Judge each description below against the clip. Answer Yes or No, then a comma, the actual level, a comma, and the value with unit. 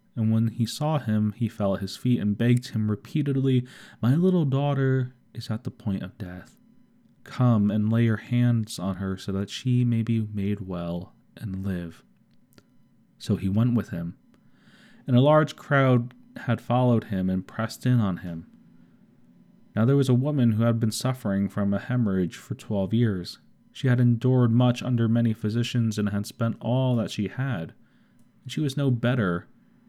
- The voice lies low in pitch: Yes, low, 115 Hz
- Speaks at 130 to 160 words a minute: No, average, 180 wpm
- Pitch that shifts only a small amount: No, average, 3.6 semitones